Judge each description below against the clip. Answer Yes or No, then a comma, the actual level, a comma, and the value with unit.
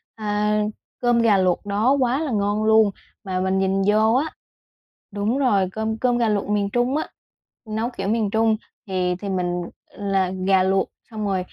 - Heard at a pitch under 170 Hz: No, high, 210 Hz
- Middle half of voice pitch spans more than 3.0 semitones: No, average, 2.7 semitones